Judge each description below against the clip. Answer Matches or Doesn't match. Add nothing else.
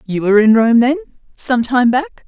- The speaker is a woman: Matches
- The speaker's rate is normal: Doesn't match